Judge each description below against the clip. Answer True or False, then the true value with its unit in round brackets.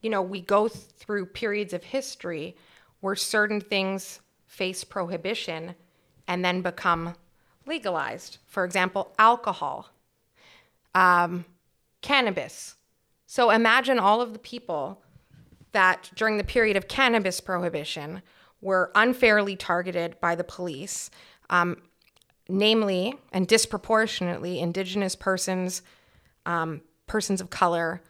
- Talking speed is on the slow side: True (110 wpm)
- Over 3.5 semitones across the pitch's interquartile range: False (3.2 semitones)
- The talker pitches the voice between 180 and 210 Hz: True (190 Hz)